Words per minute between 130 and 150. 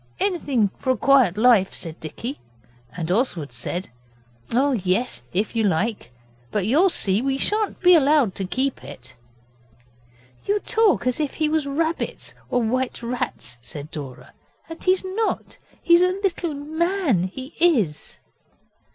Yes: average, 145 wpm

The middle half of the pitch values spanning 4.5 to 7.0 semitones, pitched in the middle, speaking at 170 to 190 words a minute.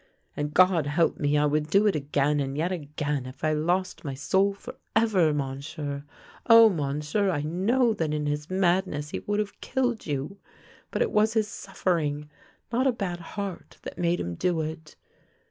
Yes: average, 5.1 semitones; medium, 160 Hz; average, 180 wpm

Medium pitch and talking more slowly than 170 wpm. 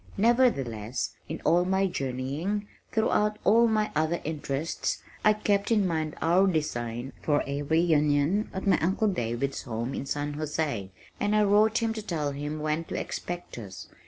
Yes: medium, 160 Hz; average, 160 wpm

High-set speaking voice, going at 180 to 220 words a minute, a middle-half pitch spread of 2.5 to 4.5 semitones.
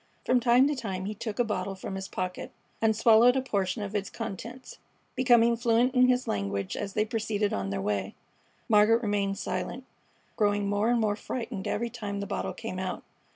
Yes: high, 210 Hz; average, 195 wpm; average, 3.4 semitones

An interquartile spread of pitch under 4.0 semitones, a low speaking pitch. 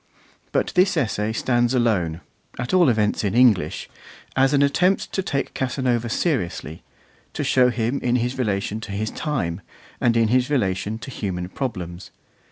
No: average, 4.3 semitones; low, 120 Hz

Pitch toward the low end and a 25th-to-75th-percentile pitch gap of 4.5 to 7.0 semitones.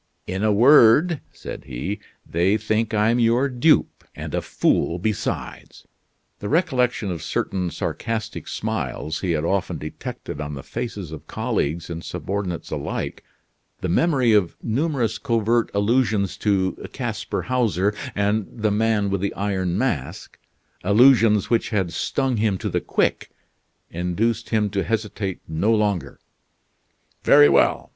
No: low, 105 Hz; average, 3.9 semitones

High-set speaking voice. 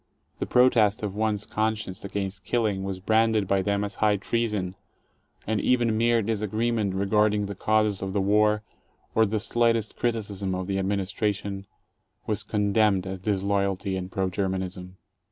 No: low, 105 Hz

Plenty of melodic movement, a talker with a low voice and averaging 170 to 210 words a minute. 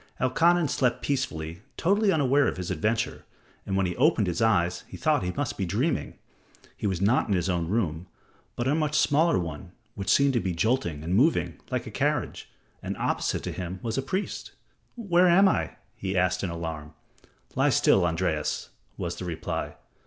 Yes: wide, 8.3 semitones; low, 100 Hz; average, 185 wpm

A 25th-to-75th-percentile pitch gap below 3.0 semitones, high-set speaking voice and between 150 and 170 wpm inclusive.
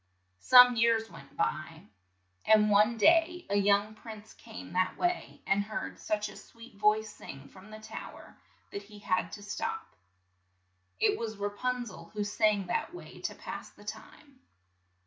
Yes: narrow, 2.4 semitones; high, 215 Hz; average, 165 wpm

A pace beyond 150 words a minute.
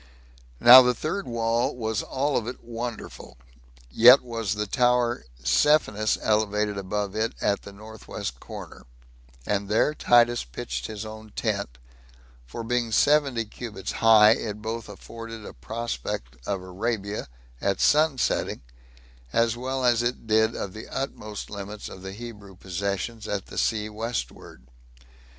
No: average, 145 wpm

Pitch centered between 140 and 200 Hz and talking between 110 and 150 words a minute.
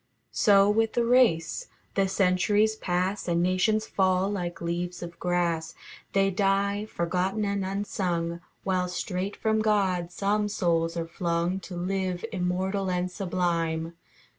Yes: medium, 185 Hz; slow, 135 wpm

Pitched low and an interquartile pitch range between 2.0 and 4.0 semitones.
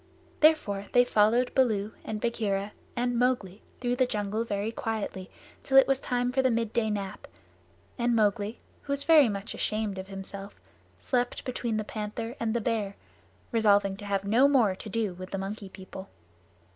No: high, 220 Hz; average, 3.4 semitones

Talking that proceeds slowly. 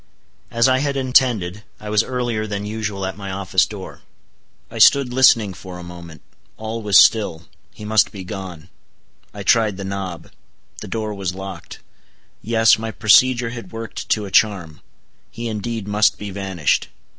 No: average, 165 wpm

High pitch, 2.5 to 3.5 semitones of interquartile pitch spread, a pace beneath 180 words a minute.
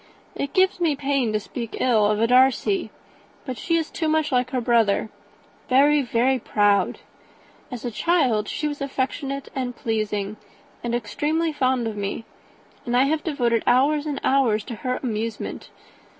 No: very high, 255 Hz; average, 4.2 semitones; average, 165 wpm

